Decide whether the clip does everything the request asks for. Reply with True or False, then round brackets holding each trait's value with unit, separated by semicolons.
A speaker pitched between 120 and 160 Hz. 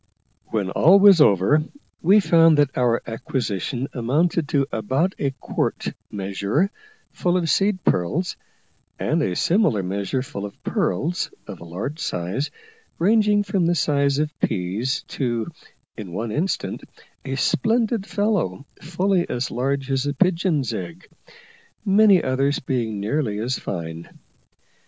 True (140 Hz)